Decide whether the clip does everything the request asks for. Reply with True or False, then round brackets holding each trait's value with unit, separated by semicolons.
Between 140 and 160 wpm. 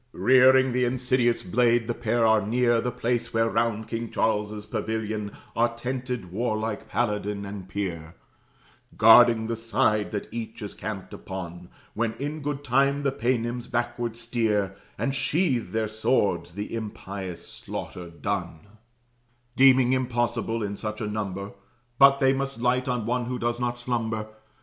True (150 wpm)